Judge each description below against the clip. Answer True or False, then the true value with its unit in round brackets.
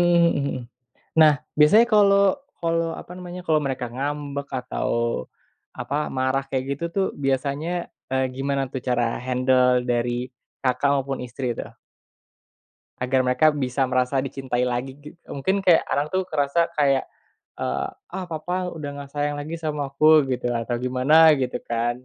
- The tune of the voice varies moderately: True (3.8 semitones)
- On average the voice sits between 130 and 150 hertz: True (140 Hz)